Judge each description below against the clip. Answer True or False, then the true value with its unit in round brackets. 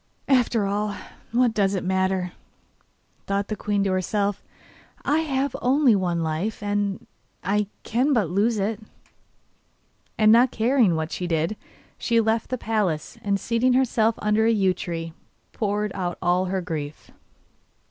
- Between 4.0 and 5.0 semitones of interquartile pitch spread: False (3.5 semitones)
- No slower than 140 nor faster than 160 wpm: True (145 wpm)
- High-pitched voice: True (205 Hz)